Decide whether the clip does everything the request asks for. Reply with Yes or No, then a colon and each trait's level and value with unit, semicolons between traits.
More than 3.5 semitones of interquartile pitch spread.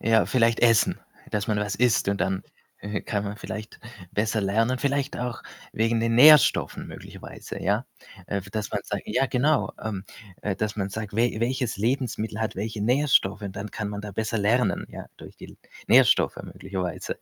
No: average, 2.7 semitones